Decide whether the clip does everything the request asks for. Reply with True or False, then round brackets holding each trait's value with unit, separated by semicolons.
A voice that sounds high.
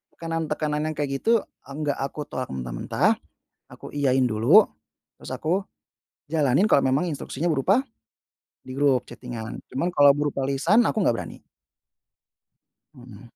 False (145 Hz)